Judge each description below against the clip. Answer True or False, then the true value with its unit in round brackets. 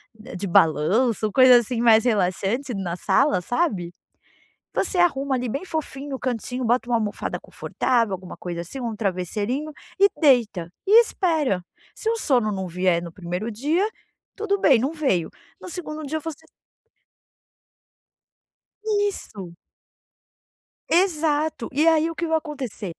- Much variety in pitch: True (7.7 semitones)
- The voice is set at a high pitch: True (245 Hz)